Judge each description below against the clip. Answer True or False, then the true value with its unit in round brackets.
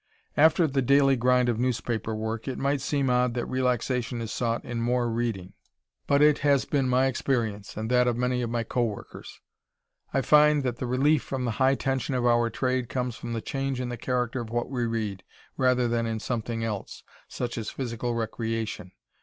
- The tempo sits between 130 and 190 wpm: False (200 wpm)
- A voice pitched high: False (125 Hz)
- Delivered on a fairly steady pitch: True (2.2 semitones)